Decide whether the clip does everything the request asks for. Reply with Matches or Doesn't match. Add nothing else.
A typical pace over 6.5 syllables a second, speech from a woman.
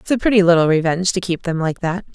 Matches